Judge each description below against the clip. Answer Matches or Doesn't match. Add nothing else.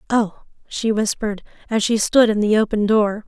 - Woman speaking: Matches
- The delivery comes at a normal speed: Matches